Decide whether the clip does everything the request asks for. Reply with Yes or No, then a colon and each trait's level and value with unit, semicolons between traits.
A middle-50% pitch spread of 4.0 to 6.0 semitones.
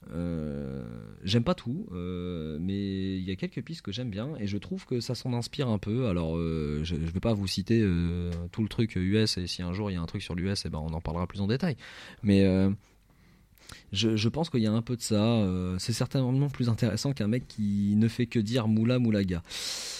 Yes: average, 4.7 semitones